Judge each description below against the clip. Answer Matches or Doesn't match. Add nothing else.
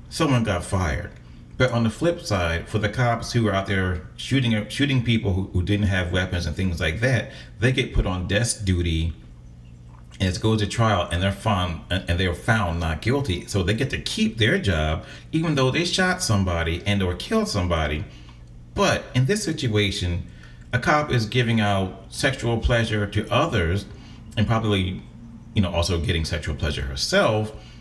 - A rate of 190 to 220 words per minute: Doesn't match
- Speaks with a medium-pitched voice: Doesn't match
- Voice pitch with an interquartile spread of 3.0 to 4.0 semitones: Doesn't match